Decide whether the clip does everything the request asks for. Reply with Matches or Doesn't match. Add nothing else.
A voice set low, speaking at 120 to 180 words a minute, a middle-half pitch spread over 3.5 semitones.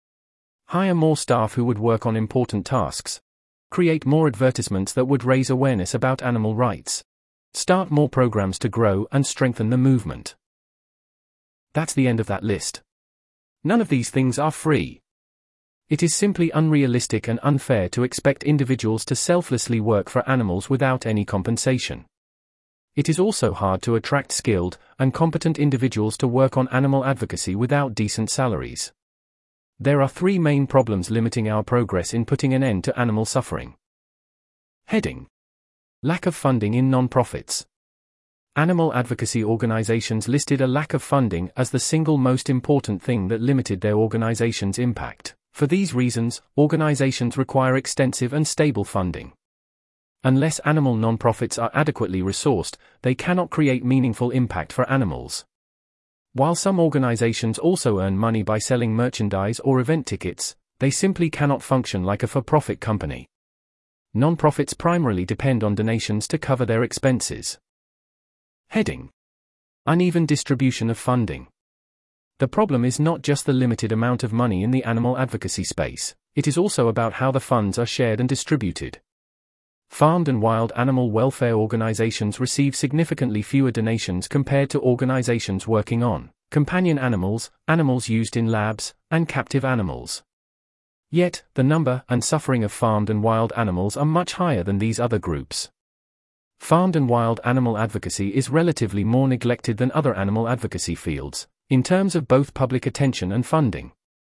Matches